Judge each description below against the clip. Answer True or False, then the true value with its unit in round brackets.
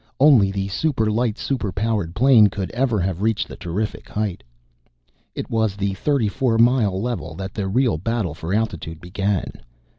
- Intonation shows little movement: False (3.3 semitones)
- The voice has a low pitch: True (105 Hz)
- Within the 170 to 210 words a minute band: True (175 wpm)